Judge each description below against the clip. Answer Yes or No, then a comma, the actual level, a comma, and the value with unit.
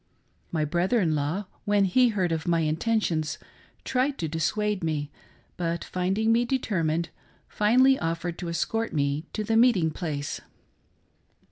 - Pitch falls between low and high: Yes, medium, 175 Hz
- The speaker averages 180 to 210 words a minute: No, average, 140 wpm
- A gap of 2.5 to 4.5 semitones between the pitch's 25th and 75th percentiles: No, wide, 5.4 semitones